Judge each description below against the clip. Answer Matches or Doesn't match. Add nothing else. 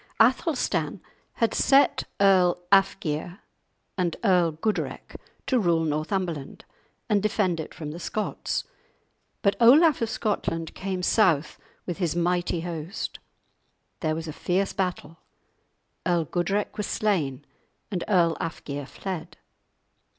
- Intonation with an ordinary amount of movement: Matches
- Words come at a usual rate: Doesn't match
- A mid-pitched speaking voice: Matches